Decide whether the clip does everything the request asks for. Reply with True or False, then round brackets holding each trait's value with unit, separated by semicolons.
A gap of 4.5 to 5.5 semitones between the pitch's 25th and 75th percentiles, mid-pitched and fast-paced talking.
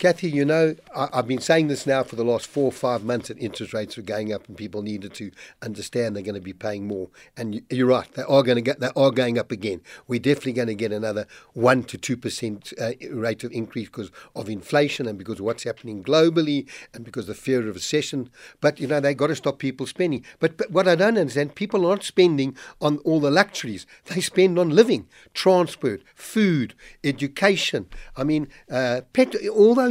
False (5.2 semitones; 130 Hz; 220 wpm)